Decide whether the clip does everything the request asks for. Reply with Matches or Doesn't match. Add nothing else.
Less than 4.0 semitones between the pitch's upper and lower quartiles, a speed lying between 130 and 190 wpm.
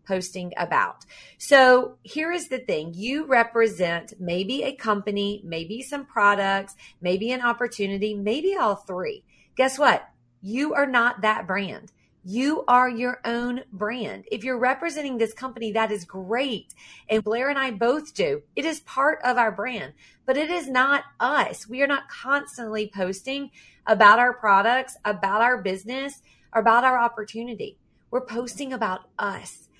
Doesn't match